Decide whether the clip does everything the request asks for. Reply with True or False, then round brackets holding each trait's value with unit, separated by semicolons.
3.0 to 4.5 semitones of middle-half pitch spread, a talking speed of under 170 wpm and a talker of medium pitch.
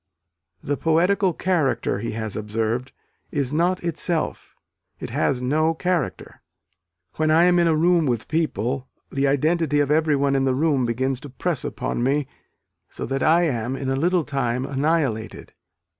True (4.1 semitones; 160 wpm; 145 Hz)